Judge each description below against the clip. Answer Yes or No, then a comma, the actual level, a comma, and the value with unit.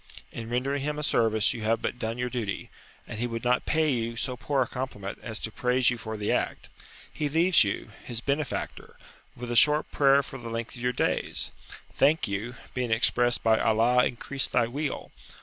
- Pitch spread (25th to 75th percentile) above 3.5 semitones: No, average, 3.0 semitones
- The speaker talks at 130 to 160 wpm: No, average, 200 wpm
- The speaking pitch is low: Yes, low, 120 Hz